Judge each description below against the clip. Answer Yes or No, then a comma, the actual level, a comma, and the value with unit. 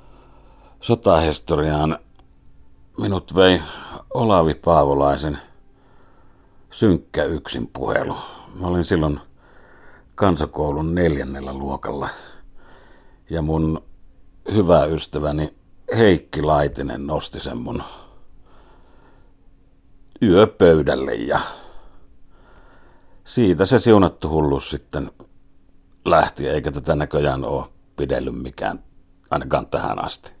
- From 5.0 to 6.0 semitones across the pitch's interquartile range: No, average, 4.1 semitones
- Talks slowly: Yes, slow, 80 wpm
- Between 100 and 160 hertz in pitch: No, very low, 75 Hz